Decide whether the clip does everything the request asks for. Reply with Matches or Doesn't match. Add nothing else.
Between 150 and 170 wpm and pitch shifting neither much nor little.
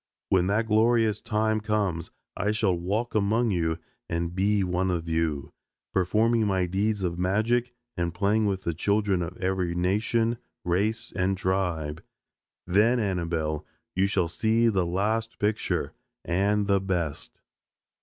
Doesn't match